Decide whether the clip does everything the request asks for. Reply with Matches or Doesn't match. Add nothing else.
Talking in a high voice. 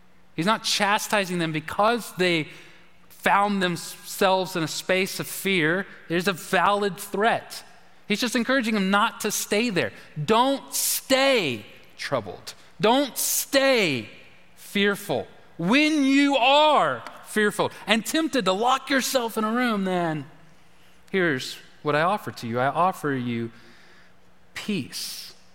Matches